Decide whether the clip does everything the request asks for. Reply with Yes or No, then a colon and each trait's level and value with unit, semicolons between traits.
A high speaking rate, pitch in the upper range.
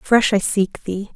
Yes: fast, 210 wpm; high, 205 Hz